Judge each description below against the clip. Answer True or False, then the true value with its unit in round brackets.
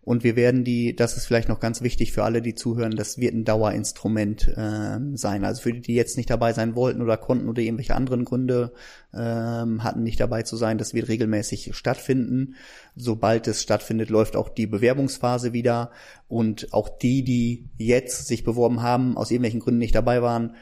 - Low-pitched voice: True (115 Hz)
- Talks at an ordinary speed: False (195 wpm)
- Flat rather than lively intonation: True (1.6 semitones)